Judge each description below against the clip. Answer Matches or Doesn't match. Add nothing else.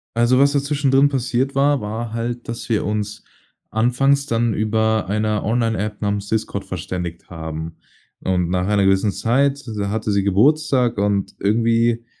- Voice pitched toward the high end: Doesn't match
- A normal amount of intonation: Matches